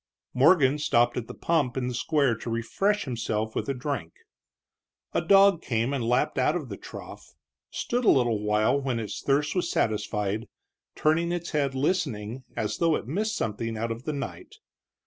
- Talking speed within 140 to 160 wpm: No, average, 180 wpm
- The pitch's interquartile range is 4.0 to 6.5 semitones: Yes, average, 5.3 semitones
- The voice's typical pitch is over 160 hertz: No, low, 130 Hz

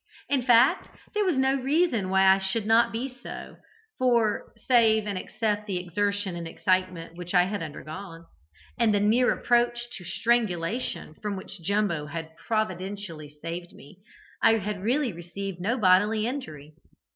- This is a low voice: No, high, 205 Hz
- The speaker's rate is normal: Yes, average, 155 wpm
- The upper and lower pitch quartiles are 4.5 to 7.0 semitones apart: Yes, average, 4.8 semitones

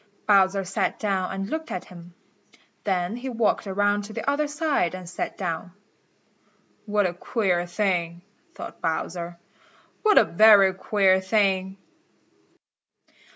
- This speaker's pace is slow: Yes, slow, 130 wpm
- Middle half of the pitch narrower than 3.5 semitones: Yes, average, 3.0 semitones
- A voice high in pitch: Yes, high, 195 Hz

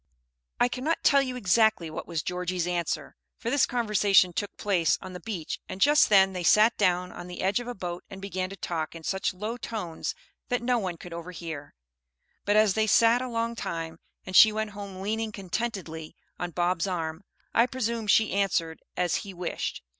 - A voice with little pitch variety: No, average, 4.1 semitones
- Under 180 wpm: No, average, 195 wpm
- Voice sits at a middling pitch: No, high, 195 Hz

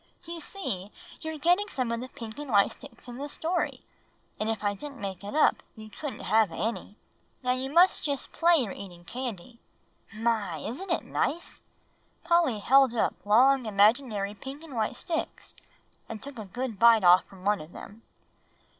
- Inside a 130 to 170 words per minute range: No, average, 180 wpm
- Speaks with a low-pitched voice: No, high, 235 Hz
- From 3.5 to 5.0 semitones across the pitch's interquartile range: No, wide, 5.4 semitones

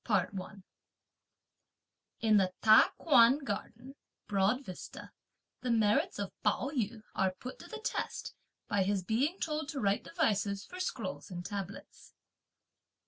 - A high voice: Yes, high, 215 Hz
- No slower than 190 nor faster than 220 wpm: No, average, 140 wpm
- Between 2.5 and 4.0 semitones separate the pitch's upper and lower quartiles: No, average, 4.8 semitones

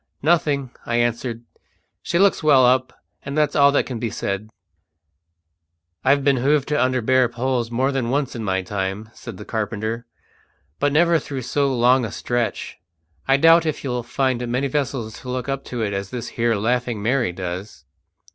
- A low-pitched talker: Yes, low, 125 Hz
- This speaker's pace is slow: No, average, 180 wpm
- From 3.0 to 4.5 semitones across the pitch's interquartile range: Yes, average, 3.3 semitones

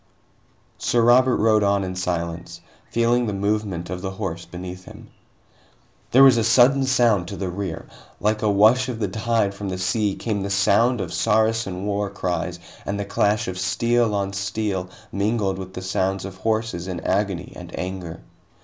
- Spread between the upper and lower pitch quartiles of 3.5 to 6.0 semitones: No, average, 3.1 semitones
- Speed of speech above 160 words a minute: Yes, average, 175 wpm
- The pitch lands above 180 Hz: No, low, 100 Hz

